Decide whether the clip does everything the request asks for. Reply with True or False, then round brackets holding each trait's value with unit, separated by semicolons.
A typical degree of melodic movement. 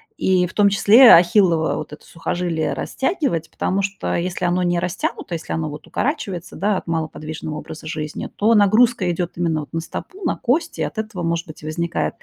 True (4.1 semitones)